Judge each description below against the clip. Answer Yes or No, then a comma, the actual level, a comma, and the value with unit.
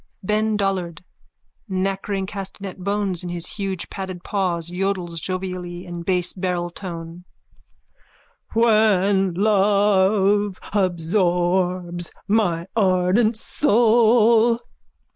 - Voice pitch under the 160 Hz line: No, high, 190 Hz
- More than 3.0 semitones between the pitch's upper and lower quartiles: No, narrow, 2.6 semitones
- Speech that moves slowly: Yes, slow, 85 wpm